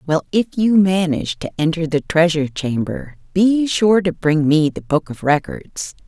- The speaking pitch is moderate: Yes, medium, 165 Hz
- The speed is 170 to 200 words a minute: Yes, average, 180 wpm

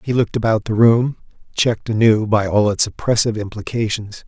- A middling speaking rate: Yes, average, 170 wpm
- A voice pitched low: Yes, low, 110 Hz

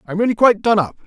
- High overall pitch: Yes, high, 205 Hz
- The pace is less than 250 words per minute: No, fast, 280 wpm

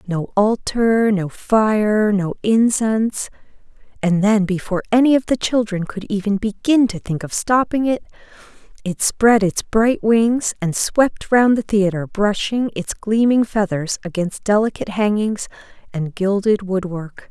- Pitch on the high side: Yes, high, 210 Hz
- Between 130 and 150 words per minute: Yes, average, 140 wpm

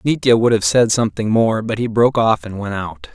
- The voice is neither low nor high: No, low, 110 Hz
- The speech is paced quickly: Yes, fast, 250 wpm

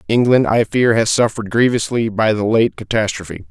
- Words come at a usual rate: Yes, average, 170 wpm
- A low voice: Yes, low, 110 Hz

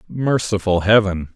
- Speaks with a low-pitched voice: Yes, low, 100 Hz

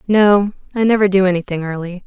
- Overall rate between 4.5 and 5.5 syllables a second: No, 5.9 syllables/s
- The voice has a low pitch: No, high, 190 Hz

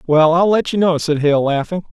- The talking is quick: Yes, fast, 240 wpm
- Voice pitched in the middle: Yes, medium, 165 Hz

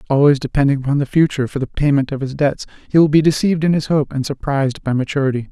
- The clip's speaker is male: Yes, male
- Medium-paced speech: No, fast, 240 wpm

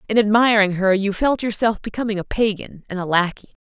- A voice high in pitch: Yes, high, 210 Hz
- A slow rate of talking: No, average, 200 wpm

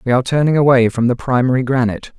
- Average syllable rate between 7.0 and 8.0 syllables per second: Yes, 7.4 syllables/s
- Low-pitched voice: Yes, low, 125 Hz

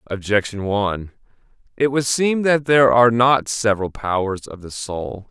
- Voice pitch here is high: No, low, 115 Hz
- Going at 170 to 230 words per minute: No, average, 160 wpm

